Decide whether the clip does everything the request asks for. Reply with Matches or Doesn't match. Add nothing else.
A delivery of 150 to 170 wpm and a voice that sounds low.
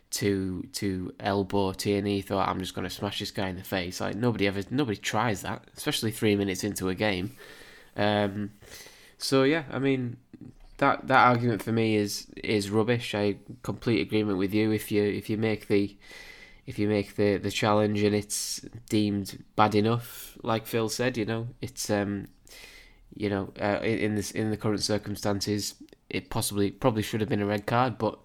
Doesn't match